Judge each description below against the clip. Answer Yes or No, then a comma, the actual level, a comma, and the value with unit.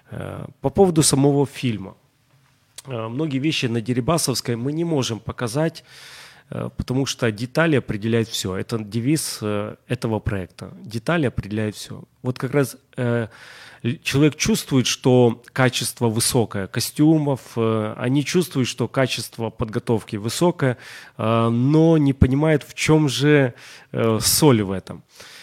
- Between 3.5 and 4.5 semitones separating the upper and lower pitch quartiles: Yes, average, 4.0 semitones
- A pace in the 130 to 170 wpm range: No, average, 115 wpm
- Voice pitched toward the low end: Yes, low, 125 Hz